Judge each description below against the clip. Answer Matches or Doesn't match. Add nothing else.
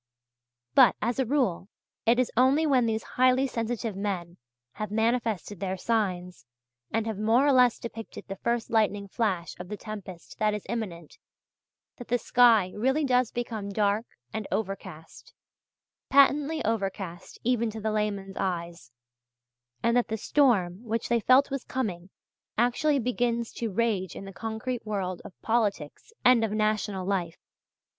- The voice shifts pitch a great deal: Doesn't match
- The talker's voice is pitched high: Matches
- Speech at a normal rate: Matches